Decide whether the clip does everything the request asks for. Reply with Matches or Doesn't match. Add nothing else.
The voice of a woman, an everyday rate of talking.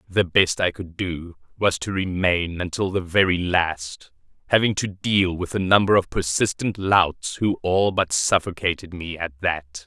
Doesn't match